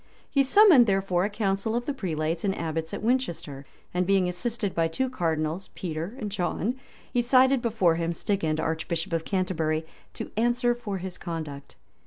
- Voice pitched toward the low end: No, high, 190 Hz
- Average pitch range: No, wide, 6.2 semitones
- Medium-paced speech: Yes, average, 170 wpm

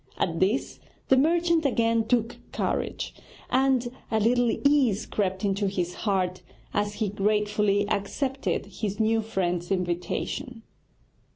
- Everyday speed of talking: No, slow, 120 wpm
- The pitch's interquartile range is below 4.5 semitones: Yes, average, 4.0 semitones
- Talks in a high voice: Yes, high, 210 Hz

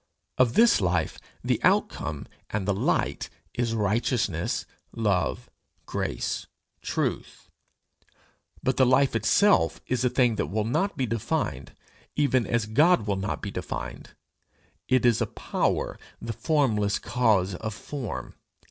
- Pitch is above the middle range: No, low, 115 Hz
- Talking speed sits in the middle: No, slow, 130 wpm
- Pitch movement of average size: Yes, average, 4.1 semitones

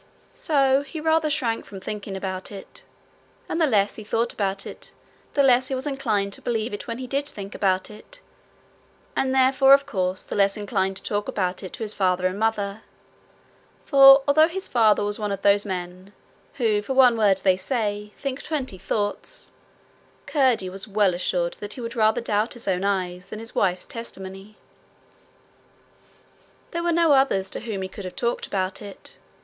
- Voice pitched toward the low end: No, high, 210 Hz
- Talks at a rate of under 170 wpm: No, average, 185 wpm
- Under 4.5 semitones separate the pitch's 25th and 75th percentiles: No, average, 5.2 semitones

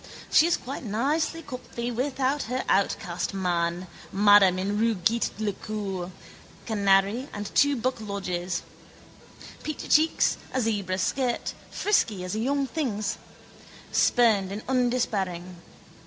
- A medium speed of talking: No, slow, 125 wpm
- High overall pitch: Yes, high, 215 Hz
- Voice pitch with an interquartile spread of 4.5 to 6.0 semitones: Yes, average, 4.9 semitones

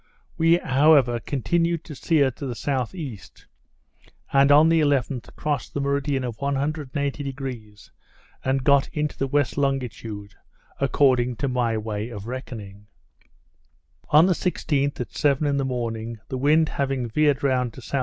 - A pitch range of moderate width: Yes, average, 3.1 semitones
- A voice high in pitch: No, low, 135 Hz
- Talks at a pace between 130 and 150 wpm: Yes, average, 145 wpm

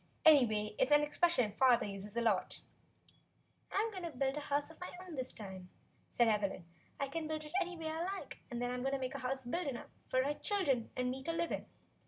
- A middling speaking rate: No, fast, 235 wpm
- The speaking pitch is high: Yes, very high, 270 Hz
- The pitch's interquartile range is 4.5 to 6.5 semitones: Yes, average, 5.0 semitones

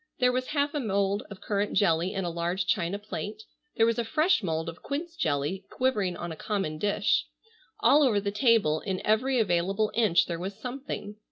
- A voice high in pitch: Yes, high, 205 Hz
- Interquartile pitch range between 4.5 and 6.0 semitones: Yes, average, 5.0 semitones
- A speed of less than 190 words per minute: No, average, 195 wpm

